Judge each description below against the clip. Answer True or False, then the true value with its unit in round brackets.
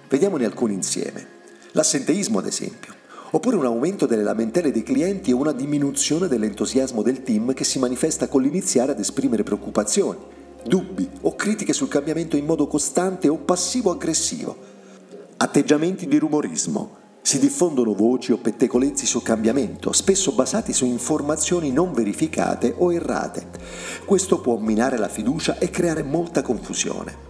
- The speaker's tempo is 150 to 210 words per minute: False (140 wpm)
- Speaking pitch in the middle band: True (145 Hz)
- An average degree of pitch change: False (6.1 semitones)